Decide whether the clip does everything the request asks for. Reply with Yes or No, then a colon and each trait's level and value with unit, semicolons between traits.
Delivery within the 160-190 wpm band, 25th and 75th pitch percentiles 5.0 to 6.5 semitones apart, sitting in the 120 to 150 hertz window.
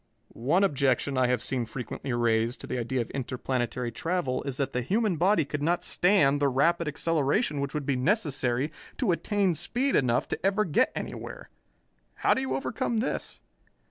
Yes: average, 175 wpm; wide, 5.6 semitones; medium, 140 Hz